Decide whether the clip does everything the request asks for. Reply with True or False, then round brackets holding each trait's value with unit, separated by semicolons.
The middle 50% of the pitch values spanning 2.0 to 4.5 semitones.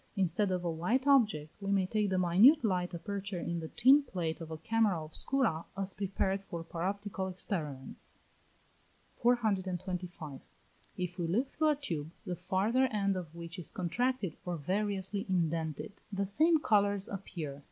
True (3.6 semitones)